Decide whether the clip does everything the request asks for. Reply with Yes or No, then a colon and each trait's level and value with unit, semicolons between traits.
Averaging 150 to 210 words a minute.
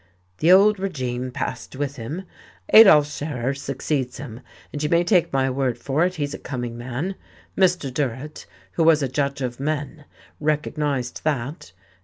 Yes: average, 160 wpm